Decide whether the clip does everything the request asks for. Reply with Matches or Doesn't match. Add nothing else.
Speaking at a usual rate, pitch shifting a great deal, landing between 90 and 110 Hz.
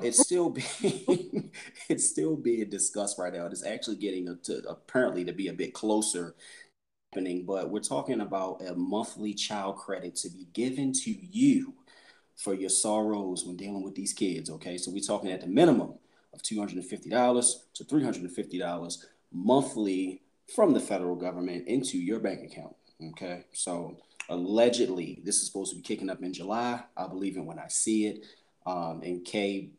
Doesn't match